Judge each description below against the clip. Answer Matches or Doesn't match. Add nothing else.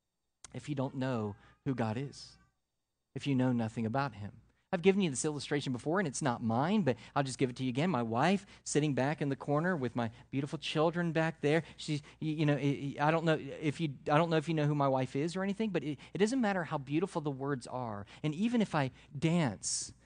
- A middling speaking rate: Doesn't match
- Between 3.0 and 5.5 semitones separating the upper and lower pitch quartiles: Matches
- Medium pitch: Matches